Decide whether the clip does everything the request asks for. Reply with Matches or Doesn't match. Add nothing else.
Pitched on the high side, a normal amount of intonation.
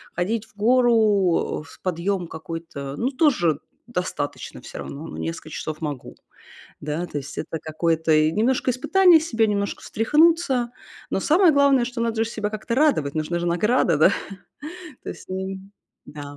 Doesn't match